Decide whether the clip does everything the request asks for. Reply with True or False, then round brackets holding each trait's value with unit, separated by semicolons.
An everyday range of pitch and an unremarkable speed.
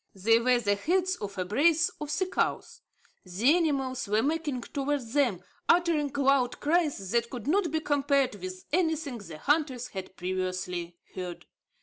False (7.2 semitones; 155 wpm)